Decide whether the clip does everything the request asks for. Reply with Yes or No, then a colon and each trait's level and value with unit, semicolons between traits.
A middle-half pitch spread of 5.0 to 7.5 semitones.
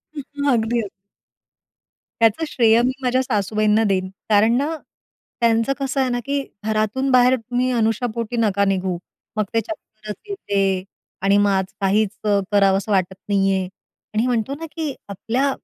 No: average, 3.9 semitones